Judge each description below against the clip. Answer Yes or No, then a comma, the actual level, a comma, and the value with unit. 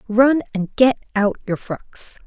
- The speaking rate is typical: Yes, average, 160 wpm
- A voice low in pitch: No, high, 225 Hz